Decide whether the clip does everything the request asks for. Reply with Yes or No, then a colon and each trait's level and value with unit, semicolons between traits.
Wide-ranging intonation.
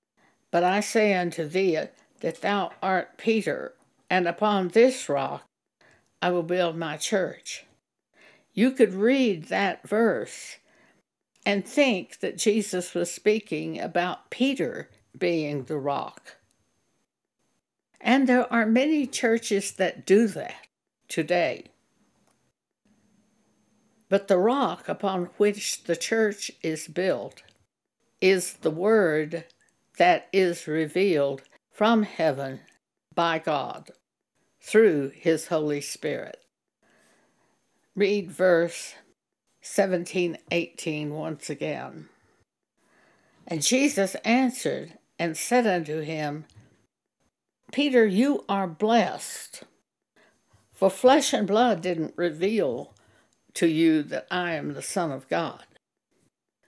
No: average, 5.0 semitones